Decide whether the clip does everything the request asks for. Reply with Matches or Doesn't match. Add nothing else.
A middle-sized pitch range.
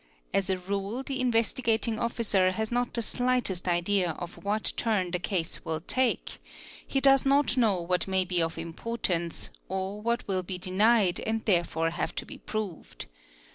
Matches